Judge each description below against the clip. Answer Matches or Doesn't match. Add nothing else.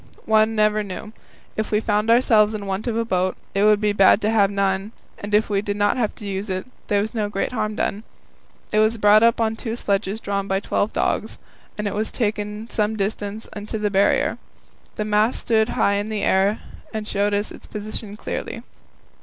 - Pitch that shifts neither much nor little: Doesn't match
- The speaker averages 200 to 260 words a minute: Matches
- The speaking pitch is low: Doesn't match